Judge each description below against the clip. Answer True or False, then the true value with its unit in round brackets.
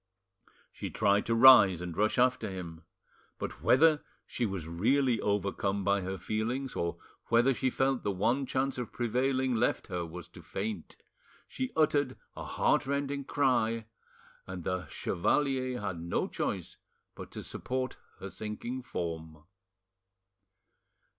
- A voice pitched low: True (115 Hz)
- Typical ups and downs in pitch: False (5.7 semitones)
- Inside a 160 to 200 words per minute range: False (135 wpm)